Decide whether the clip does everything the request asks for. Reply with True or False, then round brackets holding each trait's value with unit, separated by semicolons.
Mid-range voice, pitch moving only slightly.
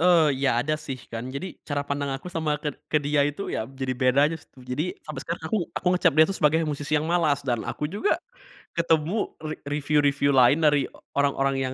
True (145 Hz; 2.3 semitones)